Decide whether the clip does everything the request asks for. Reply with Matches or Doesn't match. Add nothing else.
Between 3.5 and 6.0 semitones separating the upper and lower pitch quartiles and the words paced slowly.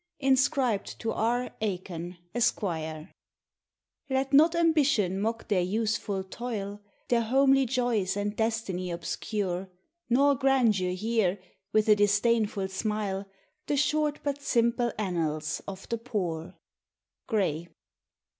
Matches